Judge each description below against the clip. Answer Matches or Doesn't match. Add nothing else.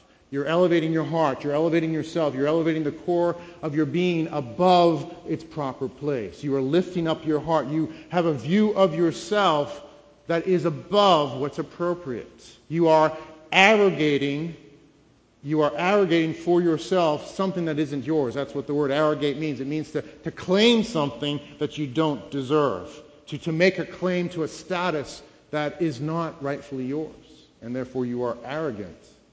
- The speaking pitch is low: Doesn't match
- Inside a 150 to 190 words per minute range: Matches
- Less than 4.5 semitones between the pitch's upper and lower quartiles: Matches